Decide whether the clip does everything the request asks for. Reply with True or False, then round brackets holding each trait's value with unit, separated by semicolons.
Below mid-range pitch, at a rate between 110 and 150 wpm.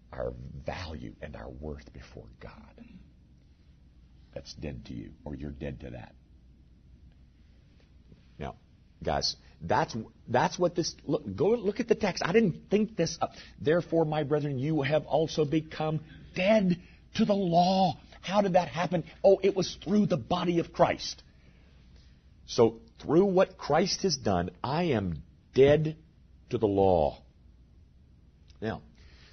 True (100 Hz; 140 wpm)